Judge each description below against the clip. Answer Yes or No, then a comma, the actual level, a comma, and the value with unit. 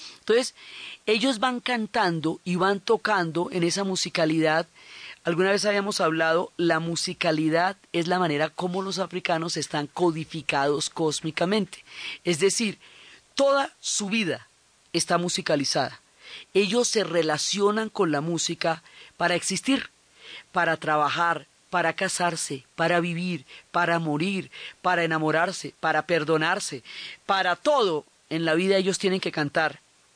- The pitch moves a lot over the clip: No, average, 3.2 semitones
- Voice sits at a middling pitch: Yes, medium, 175 Hz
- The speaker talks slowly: Yes, slow, 120 wpm